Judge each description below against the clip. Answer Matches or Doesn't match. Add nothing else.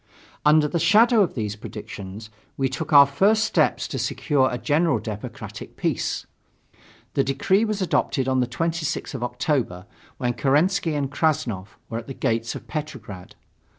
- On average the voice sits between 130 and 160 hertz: Matches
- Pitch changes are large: Matches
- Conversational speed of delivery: Matches